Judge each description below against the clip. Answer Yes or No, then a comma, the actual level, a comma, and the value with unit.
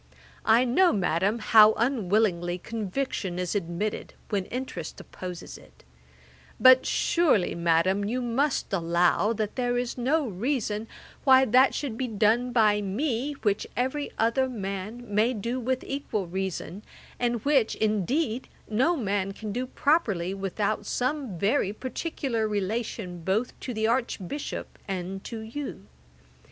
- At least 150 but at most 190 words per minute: No, slow, 135 wpm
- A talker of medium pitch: No, high, 220 Hz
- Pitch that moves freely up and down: No, average, 4.6 semitones